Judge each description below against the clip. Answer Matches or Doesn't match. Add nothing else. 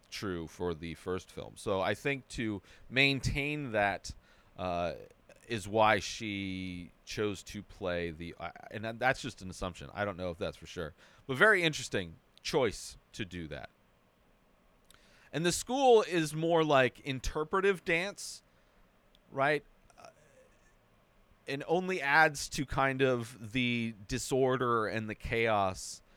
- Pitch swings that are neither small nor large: Doesn't match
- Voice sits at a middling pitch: Doesn't match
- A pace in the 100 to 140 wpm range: Matches